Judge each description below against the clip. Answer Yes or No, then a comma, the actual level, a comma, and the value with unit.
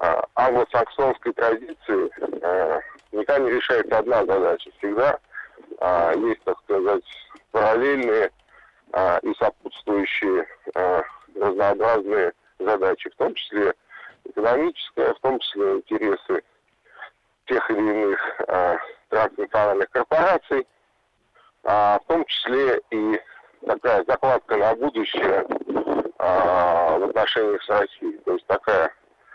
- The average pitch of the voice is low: No, very high, 395 Hz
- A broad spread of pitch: No, average, 3.3 semitones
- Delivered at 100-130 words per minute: Yes, slow, 110 wpm